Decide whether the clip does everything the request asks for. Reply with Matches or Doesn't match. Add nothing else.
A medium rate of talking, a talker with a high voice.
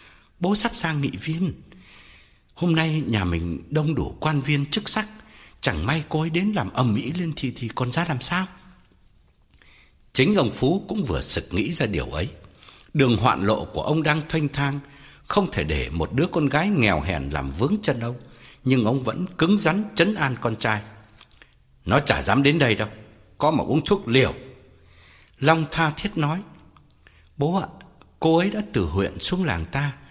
Doesn't match